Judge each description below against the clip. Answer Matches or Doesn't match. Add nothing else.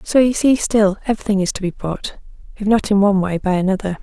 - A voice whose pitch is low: Doesn't match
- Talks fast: Matches